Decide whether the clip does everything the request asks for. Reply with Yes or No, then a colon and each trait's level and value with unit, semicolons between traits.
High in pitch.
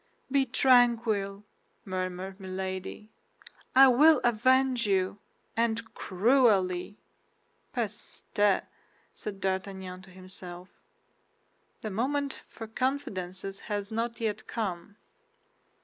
Yes: high, 205 Hz